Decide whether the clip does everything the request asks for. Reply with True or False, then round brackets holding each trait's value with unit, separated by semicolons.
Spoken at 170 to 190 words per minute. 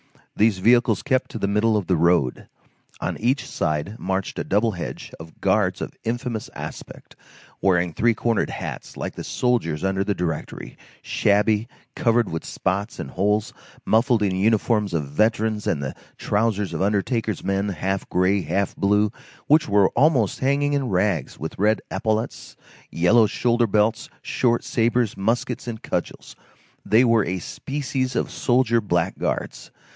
False (150 wpm)